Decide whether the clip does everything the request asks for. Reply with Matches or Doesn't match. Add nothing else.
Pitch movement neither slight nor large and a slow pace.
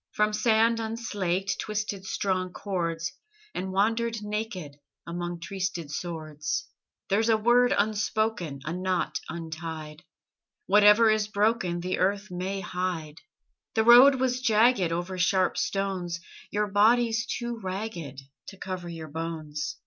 Matches